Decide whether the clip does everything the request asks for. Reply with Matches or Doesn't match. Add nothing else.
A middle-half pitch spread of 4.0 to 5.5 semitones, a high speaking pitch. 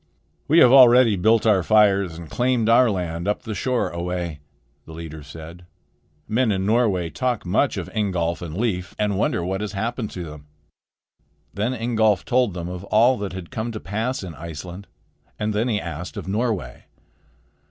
Doesn't match